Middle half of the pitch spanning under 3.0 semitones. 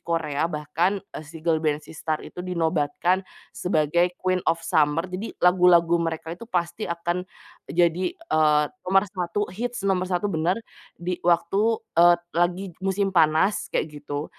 Yes: narrow, 2.6 semitones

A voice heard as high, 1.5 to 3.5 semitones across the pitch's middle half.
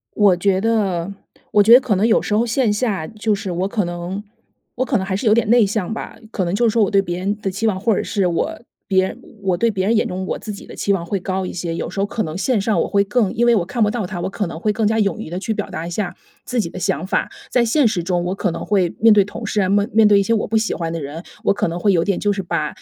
Yes: high, 200 Hz; average, 3.2 semitones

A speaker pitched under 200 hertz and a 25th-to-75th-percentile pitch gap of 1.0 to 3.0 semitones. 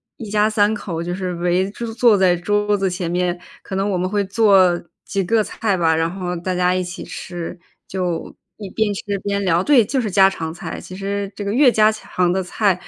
Yes: high, 190 Hz; average, 2.7 semitones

